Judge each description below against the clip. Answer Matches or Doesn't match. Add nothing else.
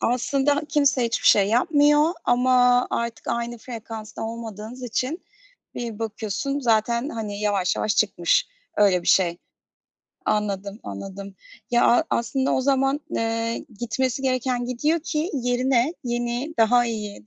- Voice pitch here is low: Doesn't match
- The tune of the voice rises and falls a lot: Doesn't match